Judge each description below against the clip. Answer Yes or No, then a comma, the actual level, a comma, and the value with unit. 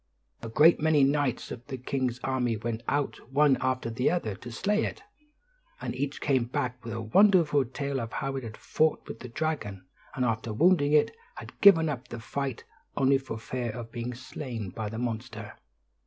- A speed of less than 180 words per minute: No, average, 190 wpm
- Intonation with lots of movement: No, average, 3.8 semitones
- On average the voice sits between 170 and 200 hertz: No, low, 130 Hz